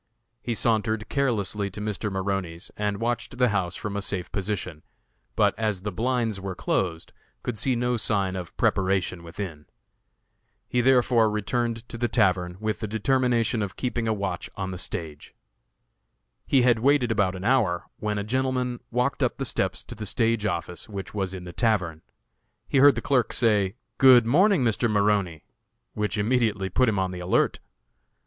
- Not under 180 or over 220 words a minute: No, average, 170 wpm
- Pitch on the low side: Yes, low, 105 Hz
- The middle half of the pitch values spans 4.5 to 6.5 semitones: No, average, 4.0 semitones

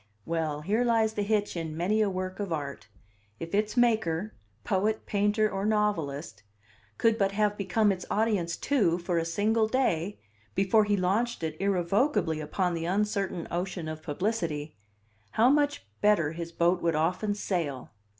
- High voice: Yes, high, 195 Hz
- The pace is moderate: Yes, average, 160 wpm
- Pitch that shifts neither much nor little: Yes, average, 4.3 semitones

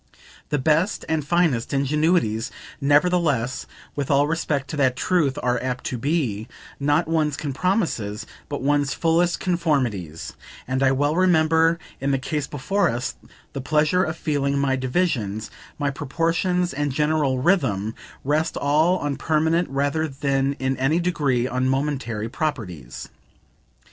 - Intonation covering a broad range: No, average, 3.6 semitones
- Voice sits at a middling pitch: Yes, medium, 145 Hz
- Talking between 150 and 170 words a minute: No, average, 140 wpm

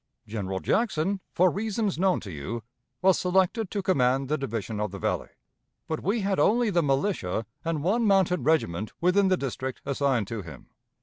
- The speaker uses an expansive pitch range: Yes, wide, 8.7 semitones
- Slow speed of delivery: No, average, 175 wpm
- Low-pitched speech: No, medium, 160 Hz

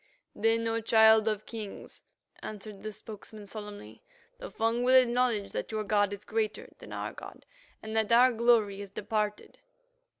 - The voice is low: No, high, 220 Hz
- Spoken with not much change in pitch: Yes, narrow, 1.7 semitones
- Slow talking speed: No, average, 160 wpm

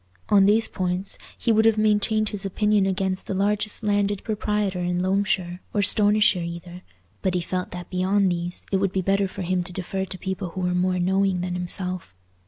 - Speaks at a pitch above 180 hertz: Yes, high, 190 Hz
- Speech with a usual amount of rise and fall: No, narrow, 2.2 semitones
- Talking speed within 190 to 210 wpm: Yes, average, 195 wpm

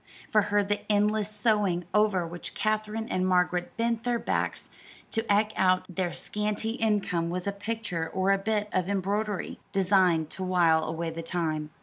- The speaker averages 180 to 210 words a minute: No, average, 165 wpm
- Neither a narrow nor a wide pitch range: Yes, average, 3.0 semitones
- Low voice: No, high, 195 Hz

